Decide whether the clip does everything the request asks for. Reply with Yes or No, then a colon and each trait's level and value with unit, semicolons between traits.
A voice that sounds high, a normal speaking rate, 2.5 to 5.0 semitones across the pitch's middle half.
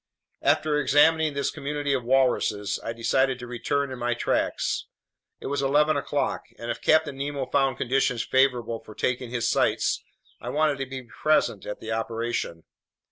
No: low, 130 Hz; average, 165 wpm; average, 3.1 semitones